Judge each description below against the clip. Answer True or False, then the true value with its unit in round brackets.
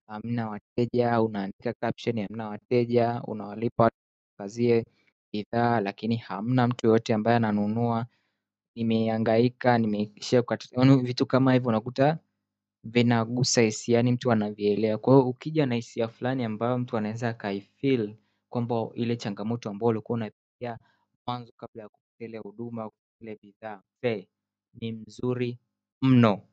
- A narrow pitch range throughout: True (2.2 semitones)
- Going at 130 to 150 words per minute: False (115 wpm)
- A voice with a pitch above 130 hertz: False (115 Hz)